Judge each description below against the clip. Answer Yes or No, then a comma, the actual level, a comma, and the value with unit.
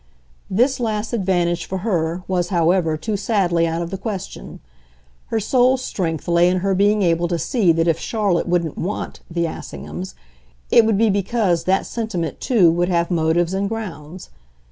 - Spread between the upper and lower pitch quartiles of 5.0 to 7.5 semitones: No, average, 3.7 semitones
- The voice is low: No, medium, 180 Hz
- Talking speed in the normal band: Yes, average, 170 wpm